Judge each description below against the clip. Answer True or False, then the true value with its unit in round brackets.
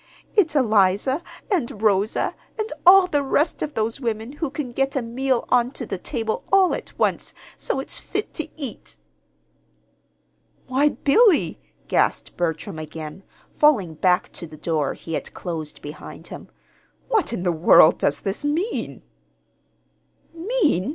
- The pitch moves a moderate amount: False (8.5 semitones)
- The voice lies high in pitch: True (240 Hz)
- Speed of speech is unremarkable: True (145 wpm)